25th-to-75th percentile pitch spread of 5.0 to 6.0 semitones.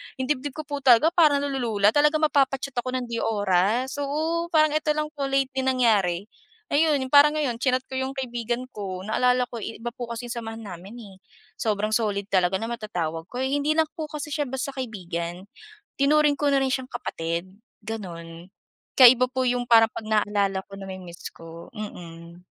Yes: wide, 5.5 semitones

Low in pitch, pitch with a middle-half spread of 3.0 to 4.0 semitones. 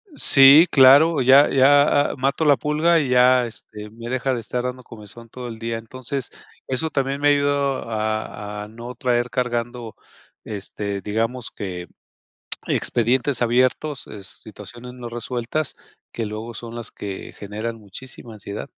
Yes: low, 120 Hz; average, 3.3 semitones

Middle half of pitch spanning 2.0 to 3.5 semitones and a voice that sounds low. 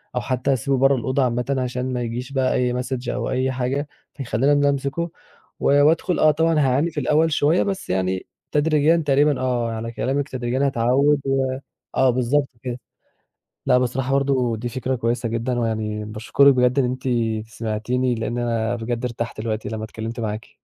Yes: average, 3.0 semitones; low, 125 Hz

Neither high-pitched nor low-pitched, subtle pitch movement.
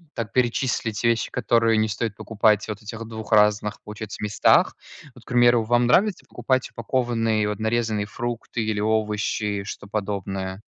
No: low, 110 Hz; narrow, 2.1 semitones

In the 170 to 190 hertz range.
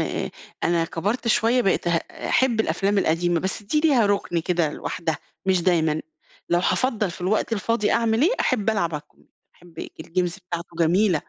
Yes: medium, 185 Hz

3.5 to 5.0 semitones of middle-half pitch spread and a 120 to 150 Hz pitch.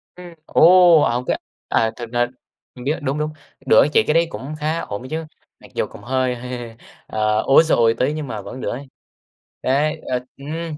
Yes: average, 4.3 semitones; low, 135 Hz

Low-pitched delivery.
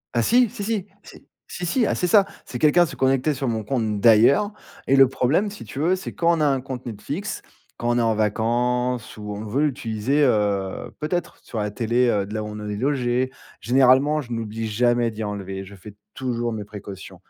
Yes: low, 120 Hz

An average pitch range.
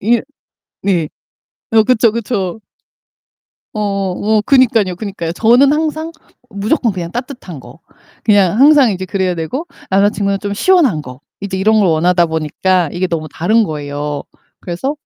Yes: average, 4.9 semitones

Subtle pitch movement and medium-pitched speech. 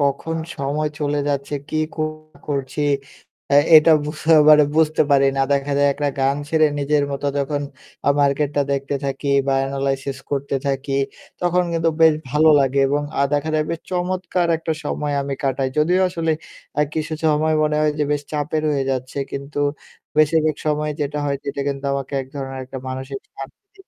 Yes: narrow, 1.9 semitones; medium, 145 Hz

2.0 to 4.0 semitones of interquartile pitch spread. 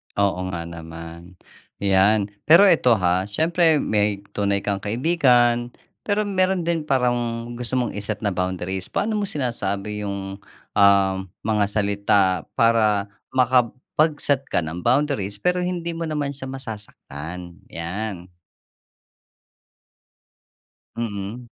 No: wide, 5.6 semitones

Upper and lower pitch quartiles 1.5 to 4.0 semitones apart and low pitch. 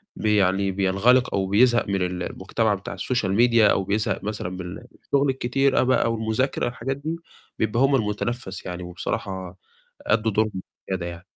No: average, 4.4 semitones; low, 105 Hz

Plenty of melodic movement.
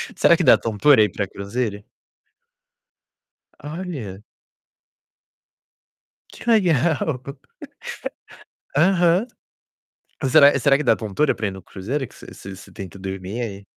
Yes: wide, 7.4 semitones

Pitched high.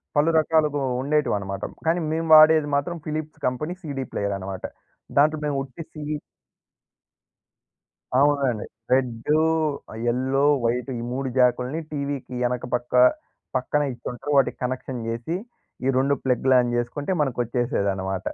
No: low, 135 Hz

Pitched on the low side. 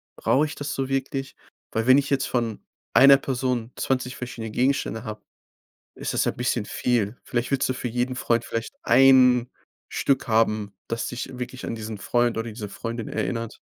Yes: low, 125 Hz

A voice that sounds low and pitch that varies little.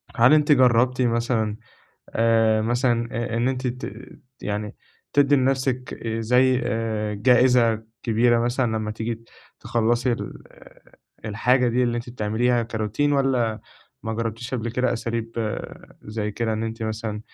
Yes: low, 115 Hz; narrow, 2.0 semitones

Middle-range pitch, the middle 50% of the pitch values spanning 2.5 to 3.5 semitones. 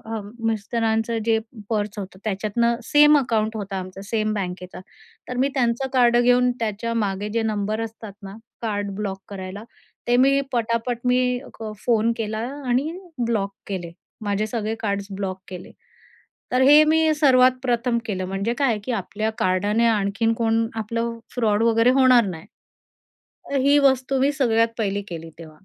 No: high, 225 Hz; average, 3.2 semitones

